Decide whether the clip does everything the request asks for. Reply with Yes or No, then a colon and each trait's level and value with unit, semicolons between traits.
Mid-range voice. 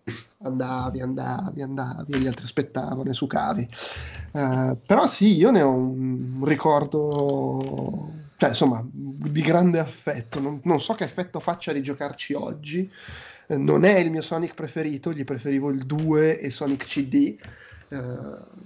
Yes: medium, 145 Hz